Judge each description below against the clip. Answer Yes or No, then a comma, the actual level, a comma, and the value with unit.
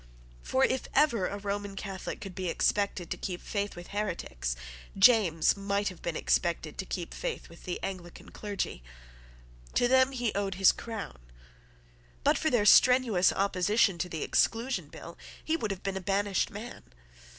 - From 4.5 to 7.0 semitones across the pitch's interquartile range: No, average, 3.3 semitones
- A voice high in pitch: Yes, high, 200 Hz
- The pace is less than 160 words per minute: No, average, 165 wpm